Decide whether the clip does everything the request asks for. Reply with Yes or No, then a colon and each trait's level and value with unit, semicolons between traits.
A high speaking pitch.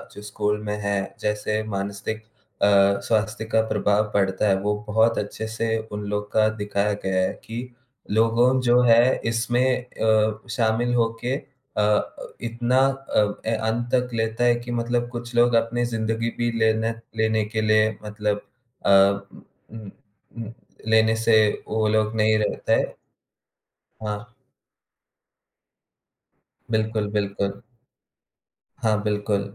No: low, 110 Hz